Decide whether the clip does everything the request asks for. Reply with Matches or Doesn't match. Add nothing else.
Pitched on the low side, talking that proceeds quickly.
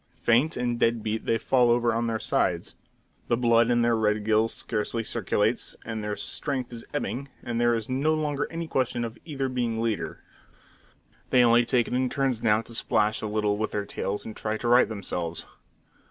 Doesn't match